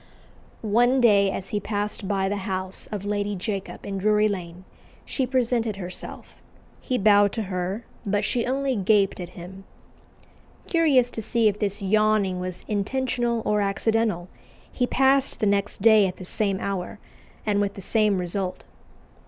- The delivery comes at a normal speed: Yes, average, 160 wpm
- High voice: Yes, high, 205 Hz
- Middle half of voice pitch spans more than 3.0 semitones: No, average, 2.7 semitones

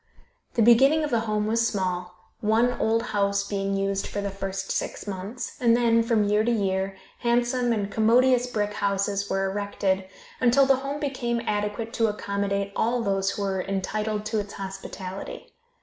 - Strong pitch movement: No, average, 3.0 semitones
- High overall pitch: Yes, high, 210 Hz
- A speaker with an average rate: Yes, average, 170 wpm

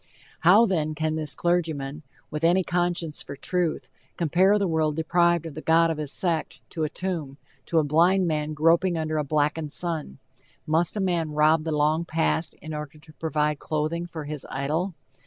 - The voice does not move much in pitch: Yes, narrow, 2.1 semitones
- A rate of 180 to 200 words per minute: Yes, average, 185 wpm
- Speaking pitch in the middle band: Yes, medium, 160 Hz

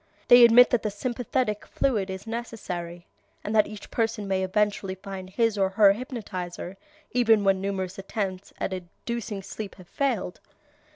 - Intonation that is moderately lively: Yes, average, 3.2 semitones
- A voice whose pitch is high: Yes, high, 205 Hz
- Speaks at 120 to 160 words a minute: Yes, average, 155 wpm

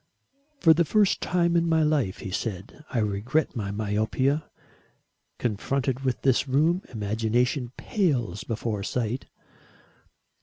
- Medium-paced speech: No, slow, 120 wpm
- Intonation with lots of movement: Yes, wide, 6.2 semitones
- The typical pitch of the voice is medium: No, low, 125 Hz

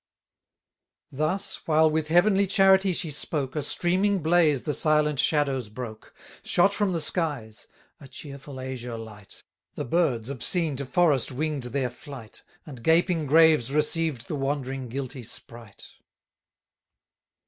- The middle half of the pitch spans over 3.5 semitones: Yes, average, 4.3 semitones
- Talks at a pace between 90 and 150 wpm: Yes, slow, 135 wpm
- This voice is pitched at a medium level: Yes, medium, 150 Hz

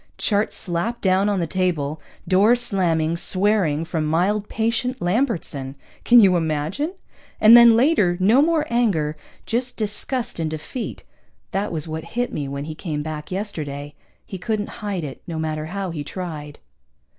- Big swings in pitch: Yes, wide, 5.8 semitones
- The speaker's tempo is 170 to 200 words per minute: No, average, 155 wpm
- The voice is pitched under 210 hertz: Yes, medium, 185 Hz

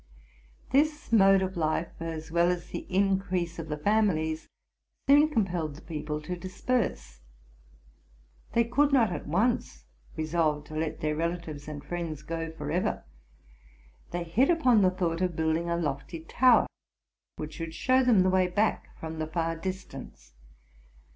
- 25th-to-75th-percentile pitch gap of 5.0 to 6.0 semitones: No, average, 3.6 semitones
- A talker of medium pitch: Yes, medium, 170 Hz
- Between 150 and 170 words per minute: Yes, average, 155 wpm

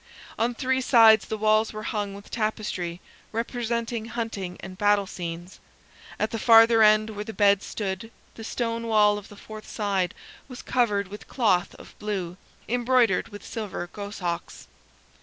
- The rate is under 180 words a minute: Yes, average, 155 wpm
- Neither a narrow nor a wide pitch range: No, narrow, 2.2 semitones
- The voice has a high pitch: Yes, high, 215 Hz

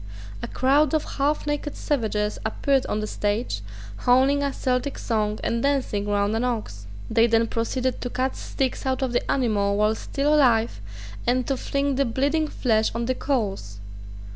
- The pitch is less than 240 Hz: No, high, 245 Hz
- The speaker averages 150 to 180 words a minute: Yes, average, 170 wpm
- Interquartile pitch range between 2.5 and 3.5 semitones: No, average, 4.2 semitones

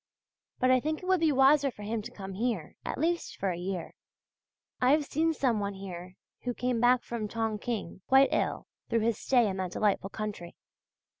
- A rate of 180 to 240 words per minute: Yes, average, 200 wpm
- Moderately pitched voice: No, high, 230 Hz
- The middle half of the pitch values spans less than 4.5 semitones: No, average, 5.2 semitones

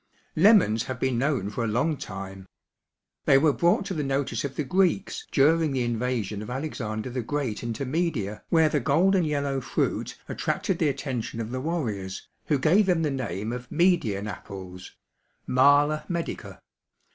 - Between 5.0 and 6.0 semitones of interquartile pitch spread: Yes, wide, 5.6 semitones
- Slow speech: No, average, 165 wpm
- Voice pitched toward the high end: No, low, 135 Hz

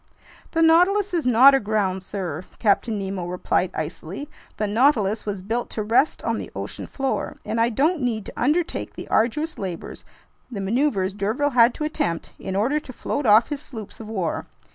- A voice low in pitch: No, high, 225 Hz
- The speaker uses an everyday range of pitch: No, wide, 6.3 semitones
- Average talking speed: Yes, average, 180 wpm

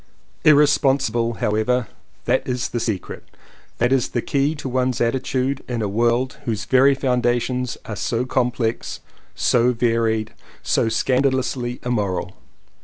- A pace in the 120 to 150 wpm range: Yes, average, 140 wpm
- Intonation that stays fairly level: Yes, narrow, 2.2 semitones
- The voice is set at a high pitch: No, low, 125 Hz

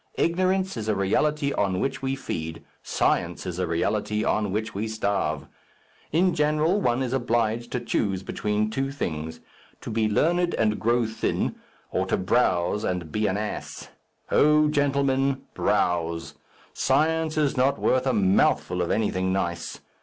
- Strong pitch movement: Yes, wide, 6.6 semitones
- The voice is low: Yes, low, 110 Hz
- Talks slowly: No, average, 155 wpm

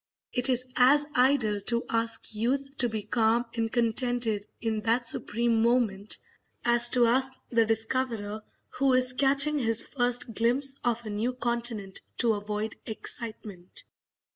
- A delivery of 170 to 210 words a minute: No, average, 140 wpm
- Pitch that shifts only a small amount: Yes, narrow, 2.3 semitones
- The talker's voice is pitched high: Yes, high, 235 Hz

